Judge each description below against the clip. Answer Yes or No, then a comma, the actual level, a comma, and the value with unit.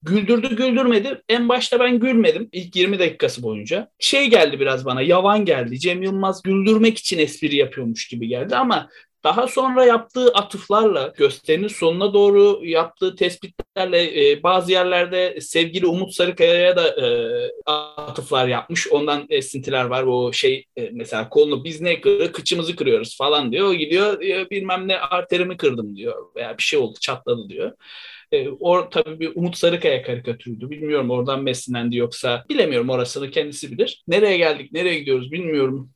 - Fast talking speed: Yes, fast, 155 wpm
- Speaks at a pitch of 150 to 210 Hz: Yes, medium, 185 Hz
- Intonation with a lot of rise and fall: Yes, wide, 8.1 semitones